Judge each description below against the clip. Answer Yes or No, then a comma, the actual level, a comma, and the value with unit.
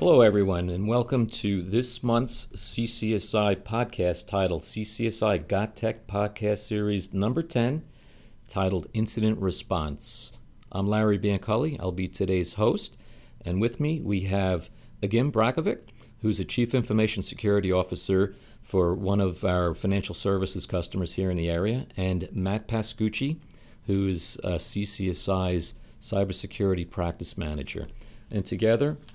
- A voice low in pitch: Yes, low, 100 Hz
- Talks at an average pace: No, slow, 130 wpm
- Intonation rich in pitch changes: No, average, 3.3 semitones